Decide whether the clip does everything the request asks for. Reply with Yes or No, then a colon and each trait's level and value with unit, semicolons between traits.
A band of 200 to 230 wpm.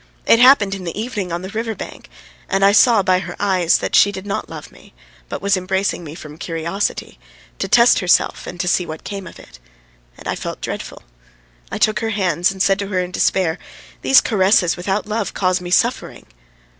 Yes: fast, 205 wpm